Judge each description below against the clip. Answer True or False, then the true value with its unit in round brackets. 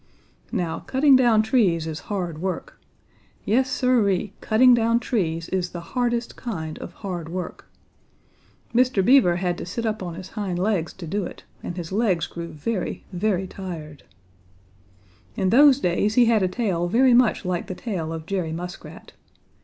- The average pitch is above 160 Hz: True (190 Hz)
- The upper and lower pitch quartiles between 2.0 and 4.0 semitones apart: False (5.0 semitones)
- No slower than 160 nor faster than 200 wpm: True (165 wpm)